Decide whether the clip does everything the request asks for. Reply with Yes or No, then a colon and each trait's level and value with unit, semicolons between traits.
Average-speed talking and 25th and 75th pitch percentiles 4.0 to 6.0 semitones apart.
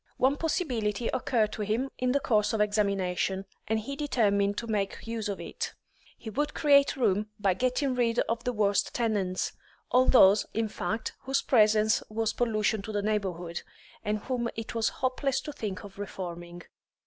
No: average, 170 wpm; average, 3.5 semitones